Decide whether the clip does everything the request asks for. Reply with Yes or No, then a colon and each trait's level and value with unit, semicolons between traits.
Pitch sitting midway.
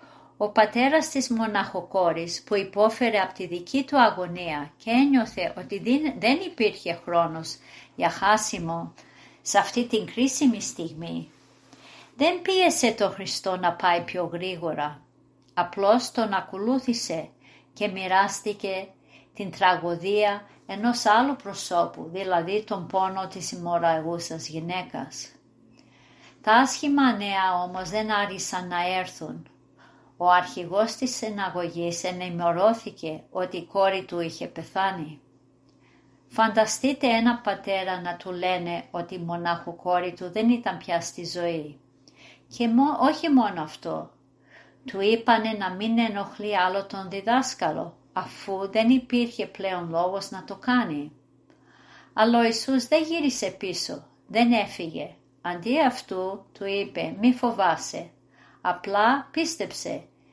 No: high, 195 Hz